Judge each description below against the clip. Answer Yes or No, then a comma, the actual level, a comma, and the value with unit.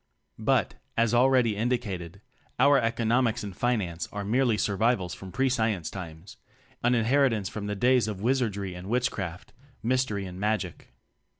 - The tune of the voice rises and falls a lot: No, average, 4.3 semitones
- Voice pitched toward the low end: Yes, low, 110 Hz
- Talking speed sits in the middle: Yes, average, 160 wpm